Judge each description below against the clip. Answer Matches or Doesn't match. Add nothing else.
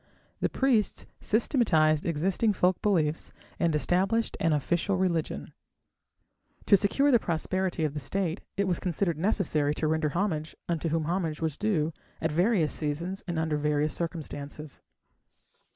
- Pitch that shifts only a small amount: Doesn't match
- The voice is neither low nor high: Matches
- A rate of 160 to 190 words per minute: Doesn't match